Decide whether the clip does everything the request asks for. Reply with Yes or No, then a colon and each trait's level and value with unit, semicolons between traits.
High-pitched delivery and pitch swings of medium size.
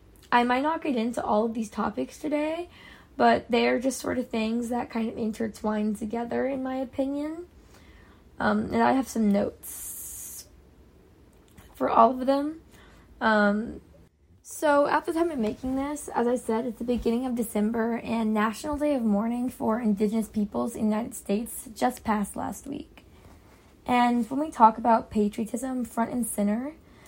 Yes: high, 235 Hz; average, 3.0 semitones